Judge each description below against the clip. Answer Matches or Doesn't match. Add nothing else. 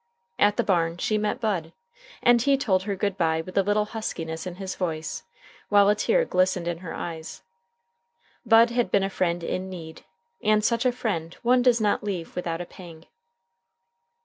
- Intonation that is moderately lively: Matches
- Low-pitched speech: Doesn't match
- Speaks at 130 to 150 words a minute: Doesn't match